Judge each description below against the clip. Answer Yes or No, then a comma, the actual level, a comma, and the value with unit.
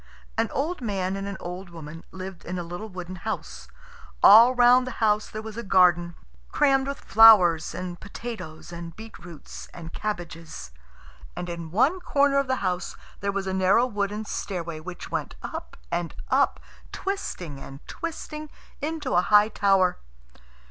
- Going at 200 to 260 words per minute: No, average, 160 wpm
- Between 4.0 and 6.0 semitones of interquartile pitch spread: Yes, average, 4.9 semitones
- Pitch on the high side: Yes, high, 195 Hz